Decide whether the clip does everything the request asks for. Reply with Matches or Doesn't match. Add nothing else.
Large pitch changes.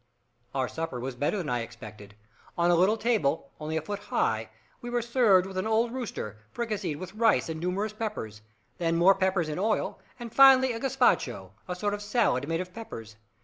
Matches